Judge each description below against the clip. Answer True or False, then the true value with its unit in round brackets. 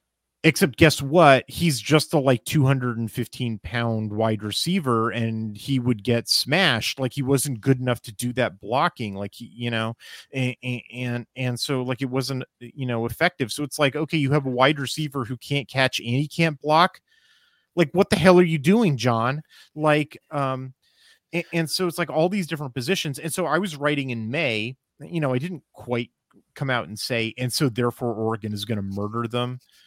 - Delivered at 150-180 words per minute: False (195 wpm)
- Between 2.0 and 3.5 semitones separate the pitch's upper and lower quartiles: False (4.6 semitones)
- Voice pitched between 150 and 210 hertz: False (130 Hz)